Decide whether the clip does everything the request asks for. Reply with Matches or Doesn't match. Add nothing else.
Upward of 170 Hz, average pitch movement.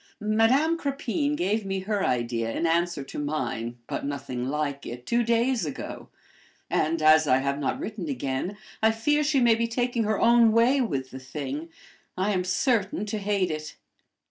Doesn't match